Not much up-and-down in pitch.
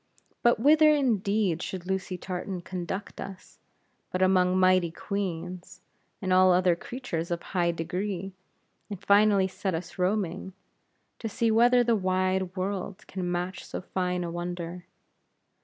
Yes: narrow, 2.1 semitones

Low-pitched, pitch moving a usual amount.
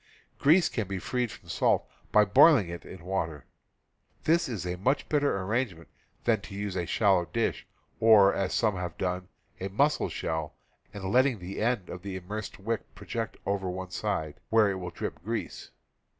Yes: low, 100 Hz; average, 3.9 semitones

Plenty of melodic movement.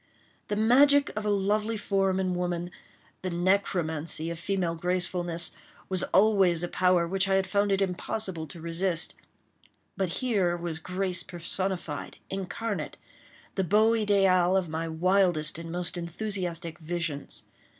No: narrow, 2.6 semitones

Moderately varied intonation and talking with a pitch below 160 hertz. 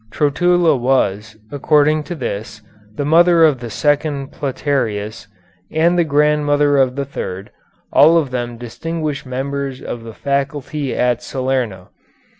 Yes: average, 3.7 semitones; medium, 140 Hz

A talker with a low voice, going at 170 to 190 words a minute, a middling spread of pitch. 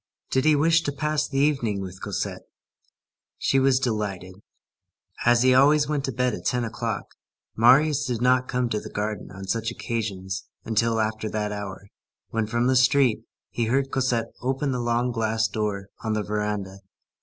Yes: low, 115 Hz; average, 175 wpm; average, 3.8 semitones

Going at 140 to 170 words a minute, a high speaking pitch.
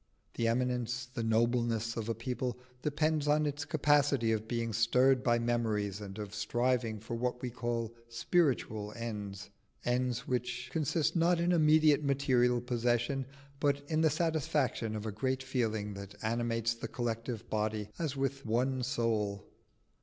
No: average, 150 wpm; low, 120 Hz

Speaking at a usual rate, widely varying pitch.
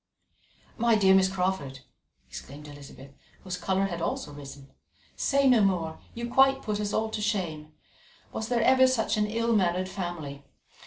Yes: average, 160 wpm; wide, 5.7 semitones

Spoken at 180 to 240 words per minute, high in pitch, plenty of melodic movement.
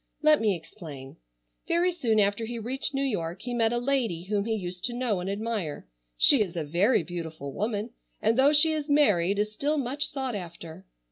Yes: average, 200 wpm; high, 215 Hz; wide, 6.7 semitones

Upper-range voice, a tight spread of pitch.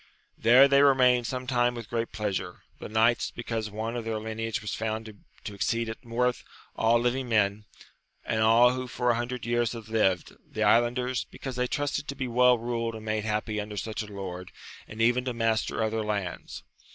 No: low, 115 Hz; narrow, 2.2 semitones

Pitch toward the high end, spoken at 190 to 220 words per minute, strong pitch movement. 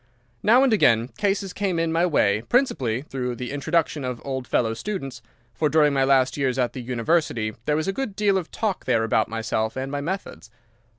No: medium, 140 Hz; average, 200 wpm; wide, 6.6 semitones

